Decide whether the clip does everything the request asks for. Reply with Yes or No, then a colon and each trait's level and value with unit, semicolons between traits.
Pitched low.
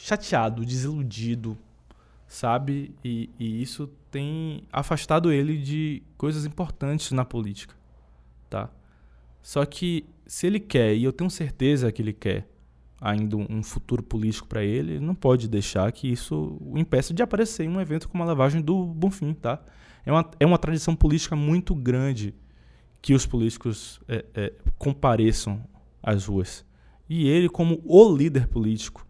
Yes: low, 130 Hz